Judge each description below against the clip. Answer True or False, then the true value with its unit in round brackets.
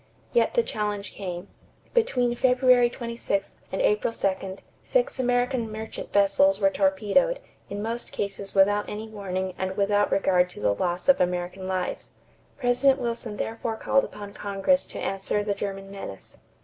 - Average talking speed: True (150 wpm)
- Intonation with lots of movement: False (3.8 semitones)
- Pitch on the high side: True (205 Hz)